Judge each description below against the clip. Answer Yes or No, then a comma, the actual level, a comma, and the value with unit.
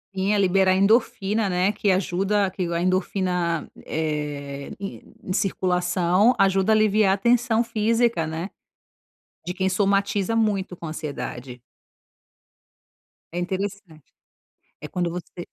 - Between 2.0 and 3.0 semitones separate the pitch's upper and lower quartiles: Yes, narrow, 2.5 semitones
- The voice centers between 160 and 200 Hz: Yes, high, 190 Hz